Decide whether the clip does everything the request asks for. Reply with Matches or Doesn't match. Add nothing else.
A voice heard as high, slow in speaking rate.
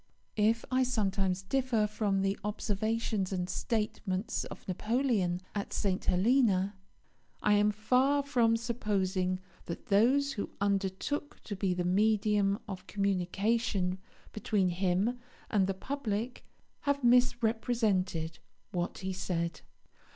Matches